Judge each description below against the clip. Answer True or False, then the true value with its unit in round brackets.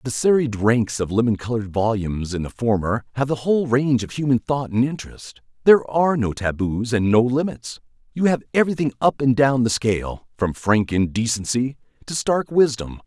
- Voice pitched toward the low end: True (120 Hz)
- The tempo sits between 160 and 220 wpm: True (185 wpm)